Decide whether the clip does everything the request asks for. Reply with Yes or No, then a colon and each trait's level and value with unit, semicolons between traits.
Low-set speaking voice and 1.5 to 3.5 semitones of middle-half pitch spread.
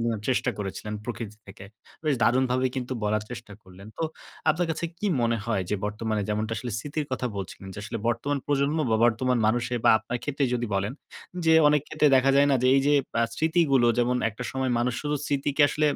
No: low, 125 Hz; average, 4.6 semitones